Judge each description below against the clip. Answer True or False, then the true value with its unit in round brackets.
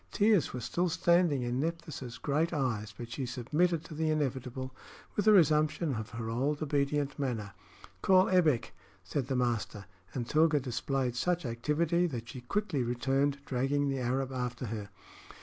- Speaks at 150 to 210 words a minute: True (160 wpm)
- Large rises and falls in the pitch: False (4.3 semitones)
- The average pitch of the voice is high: False (135 Hz)